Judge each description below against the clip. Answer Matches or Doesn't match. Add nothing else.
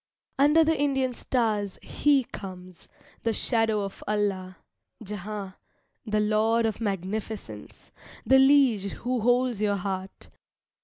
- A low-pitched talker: Doesn't match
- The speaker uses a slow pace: Matches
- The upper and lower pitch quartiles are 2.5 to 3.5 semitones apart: Doesn't match